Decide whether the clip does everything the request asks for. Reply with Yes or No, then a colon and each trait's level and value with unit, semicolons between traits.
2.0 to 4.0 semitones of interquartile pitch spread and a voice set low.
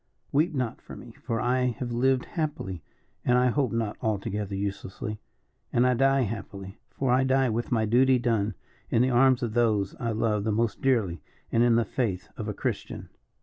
Yes: average, 3.2 semitones; low, 120 Hz